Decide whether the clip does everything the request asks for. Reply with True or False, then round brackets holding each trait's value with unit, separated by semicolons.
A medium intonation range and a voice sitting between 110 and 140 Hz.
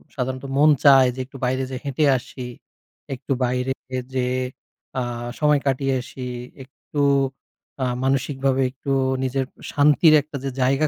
False (1.5 semitones; 135 Hz)